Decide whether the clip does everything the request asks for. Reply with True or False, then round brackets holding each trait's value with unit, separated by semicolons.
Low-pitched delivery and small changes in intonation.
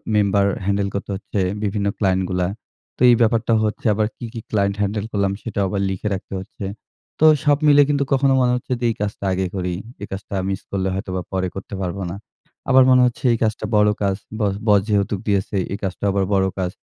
True (100 Hz; 2.2 semitones)